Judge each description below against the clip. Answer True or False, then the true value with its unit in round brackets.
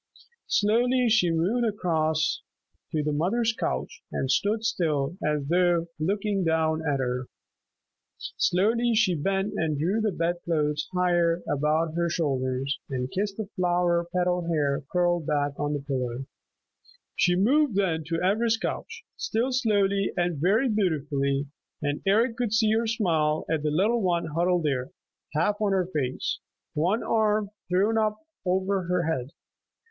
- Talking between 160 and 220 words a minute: False (150 wpm)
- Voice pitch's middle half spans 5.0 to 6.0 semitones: True (5.4 semitones)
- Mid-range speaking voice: True (175 Hz)